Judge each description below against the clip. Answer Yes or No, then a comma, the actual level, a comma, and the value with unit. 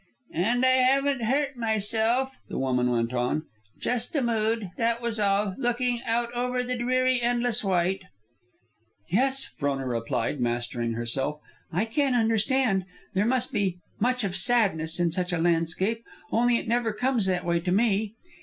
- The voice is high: Yes, high, 220 Hz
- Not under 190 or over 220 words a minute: No, average, 155 wpm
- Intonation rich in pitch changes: Yes, wide, 6.0 semitones